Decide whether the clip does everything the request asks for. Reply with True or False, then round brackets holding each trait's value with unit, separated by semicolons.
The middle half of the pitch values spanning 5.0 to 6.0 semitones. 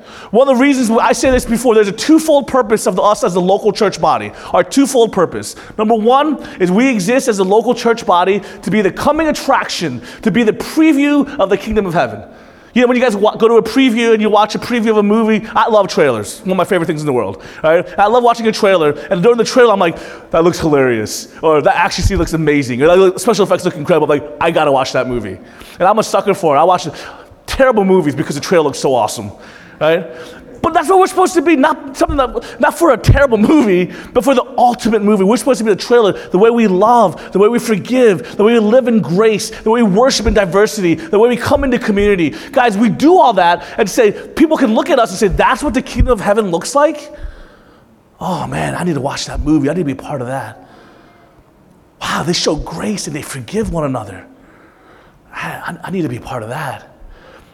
True (5.3 semitones)